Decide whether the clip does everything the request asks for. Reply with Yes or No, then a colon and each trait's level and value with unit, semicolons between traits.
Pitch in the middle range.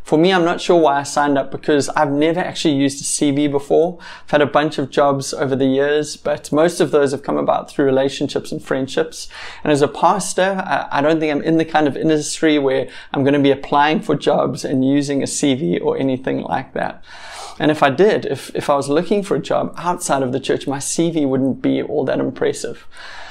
Yes: medium, 145 Hz